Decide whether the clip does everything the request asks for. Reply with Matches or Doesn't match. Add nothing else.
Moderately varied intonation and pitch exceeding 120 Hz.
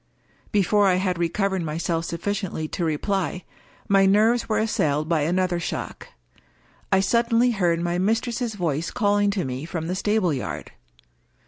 Matches